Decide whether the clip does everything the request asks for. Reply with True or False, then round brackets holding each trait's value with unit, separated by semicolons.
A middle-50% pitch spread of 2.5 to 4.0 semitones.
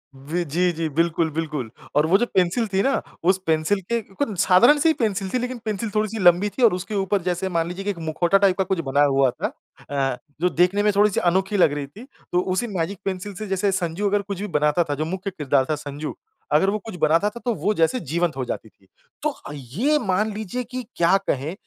False (4.5 semitones)